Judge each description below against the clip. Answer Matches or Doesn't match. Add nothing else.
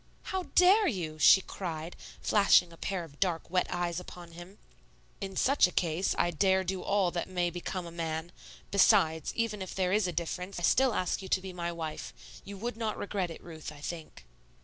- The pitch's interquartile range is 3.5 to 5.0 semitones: Doesn't match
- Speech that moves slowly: Doesn't match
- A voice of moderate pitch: Matches